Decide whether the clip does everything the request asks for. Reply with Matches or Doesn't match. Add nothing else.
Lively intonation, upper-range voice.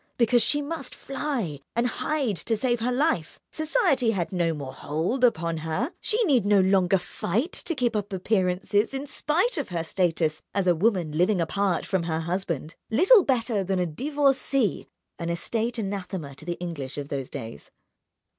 Matches